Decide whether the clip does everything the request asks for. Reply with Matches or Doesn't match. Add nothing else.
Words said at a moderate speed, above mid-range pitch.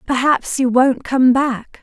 Matches